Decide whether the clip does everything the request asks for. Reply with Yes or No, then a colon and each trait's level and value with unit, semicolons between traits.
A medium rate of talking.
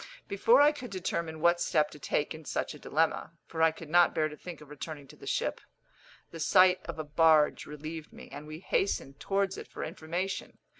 No: fast, 210 wpm